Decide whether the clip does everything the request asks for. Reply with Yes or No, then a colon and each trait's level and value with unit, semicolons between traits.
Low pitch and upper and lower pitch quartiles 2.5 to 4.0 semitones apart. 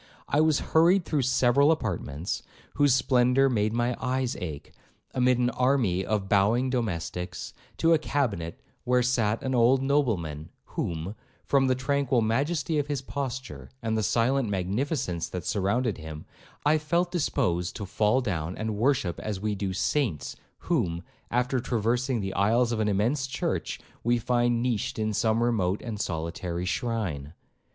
No: low, 120 Hz; average, 5.2 semitones